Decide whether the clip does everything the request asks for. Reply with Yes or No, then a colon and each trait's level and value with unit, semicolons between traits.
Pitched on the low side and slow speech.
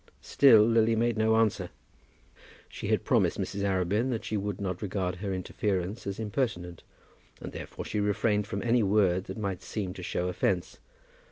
No: low, 100 Hz; average, 170 wpm